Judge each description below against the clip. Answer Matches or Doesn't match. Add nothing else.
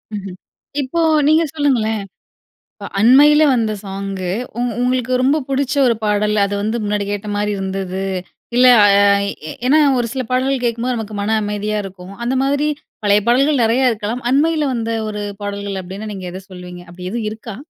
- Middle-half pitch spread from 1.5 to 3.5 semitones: Doesn't match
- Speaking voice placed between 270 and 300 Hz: Doesn't match